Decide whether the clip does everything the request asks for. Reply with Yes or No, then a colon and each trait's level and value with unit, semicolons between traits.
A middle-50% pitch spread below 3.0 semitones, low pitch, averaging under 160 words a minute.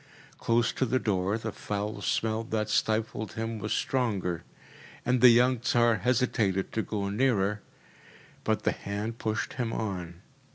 Yes: narrow, 2.6 semitones; low, 110 Hz; average, 150 wpm